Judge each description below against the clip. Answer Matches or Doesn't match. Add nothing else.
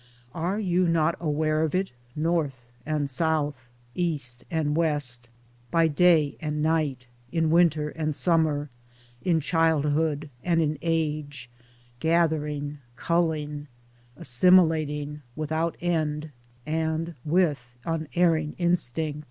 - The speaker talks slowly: Matches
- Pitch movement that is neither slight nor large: Doesn't match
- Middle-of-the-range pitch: Matches